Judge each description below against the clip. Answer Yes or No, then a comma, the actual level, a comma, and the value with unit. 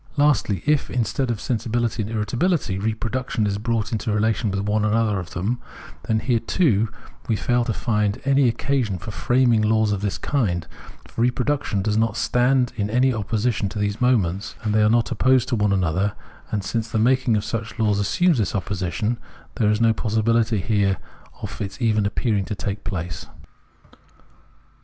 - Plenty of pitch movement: No, average, 2.8 semitones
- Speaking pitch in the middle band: No, low, 110 Hz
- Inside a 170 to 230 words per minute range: Yes, average, 175 wpm